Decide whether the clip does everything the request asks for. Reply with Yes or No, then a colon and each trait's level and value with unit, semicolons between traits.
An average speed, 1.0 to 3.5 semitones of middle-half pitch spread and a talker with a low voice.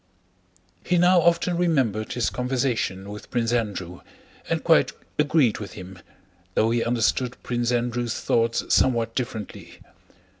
No: slow, 125 wpm; average, 3.2 semitones; low, 120 Hz